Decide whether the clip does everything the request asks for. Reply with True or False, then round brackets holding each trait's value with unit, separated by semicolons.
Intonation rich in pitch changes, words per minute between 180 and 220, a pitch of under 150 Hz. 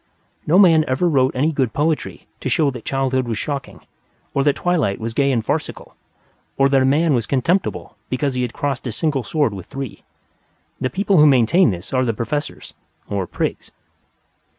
False (3.4 semitones; 185 wpm; 135 Hz)